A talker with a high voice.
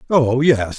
No: low, 130 Hz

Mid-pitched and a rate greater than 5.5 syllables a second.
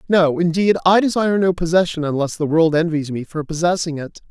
Yes: medium, 170 Hz; 5.8 syllables/s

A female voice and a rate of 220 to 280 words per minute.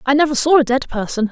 Yes: female; fast, 275 wpm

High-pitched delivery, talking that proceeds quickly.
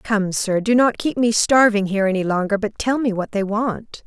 Yes: high, 215 Hz; fast, 235 wpm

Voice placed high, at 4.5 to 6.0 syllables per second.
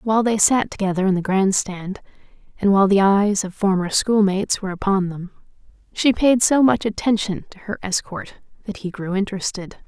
Yes: high, 200 Hz; 5.4 syllables/s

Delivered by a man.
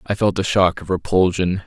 Yes: male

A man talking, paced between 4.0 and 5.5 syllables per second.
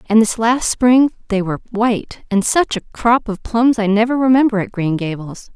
No: female; 5.0 syllables/s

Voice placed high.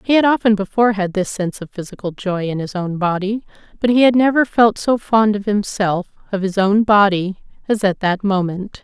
Yes: high, 205 Hz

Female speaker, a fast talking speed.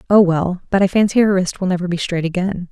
Yes: female; fast, 265 wpm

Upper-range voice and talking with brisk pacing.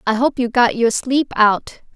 Yes: high, 240 Hz; fast, 215 wpm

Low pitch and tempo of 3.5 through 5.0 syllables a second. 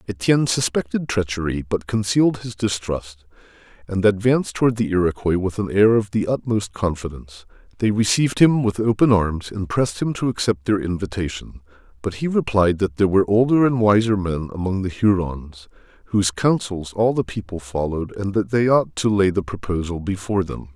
No: low, 100 Hz; 5.6 syllables/s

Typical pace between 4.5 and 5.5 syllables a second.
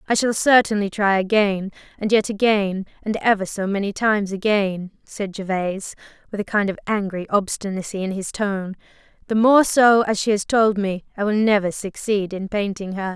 Yes: 5.0 syllables/s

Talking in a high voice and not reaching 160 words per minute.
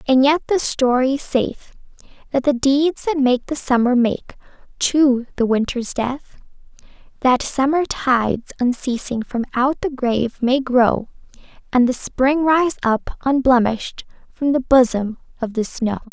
Yes: very high, 260 Hz; average, 145 wpm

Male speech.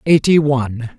Yes: male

